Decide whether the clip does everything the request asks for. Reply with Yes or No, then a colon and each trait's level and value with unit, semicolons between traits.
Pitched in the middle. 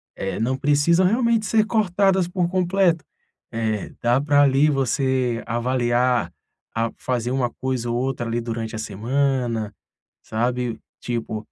No: low, 130 Hz